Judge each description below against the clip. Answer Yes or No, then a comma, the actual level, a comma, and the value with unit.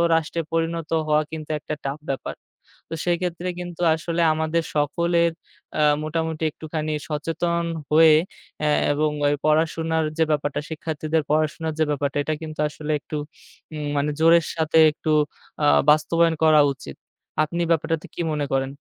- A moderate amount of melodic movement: No, narrow, 1.5 semitones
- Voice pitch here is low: No, medium, 155 Hz